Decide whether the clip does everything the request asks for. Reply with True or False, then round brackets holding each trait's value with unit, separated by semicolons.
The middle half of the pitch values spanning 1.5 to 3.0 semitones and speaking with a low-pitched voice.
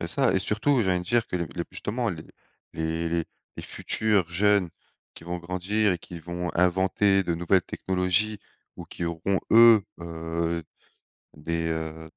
False (3.5 semitones; 90 Hz)